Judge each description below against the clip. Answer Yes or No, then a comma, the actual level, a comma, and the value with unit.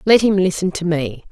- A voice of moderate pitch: Yes, medium, 180 Hz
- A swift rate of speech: Yes, fast, 230 wpm